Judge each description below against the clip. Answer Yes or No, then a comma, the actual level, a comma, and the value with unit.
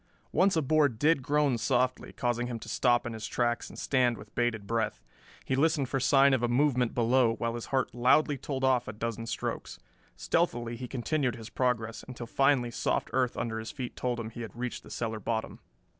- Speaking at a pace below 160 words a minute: No, fast, 205 wpm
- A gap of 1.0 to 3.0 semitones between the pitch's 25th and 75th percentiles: Yes, narrow, 2.4 semitones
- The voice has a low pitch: Yes, low, 120 Hz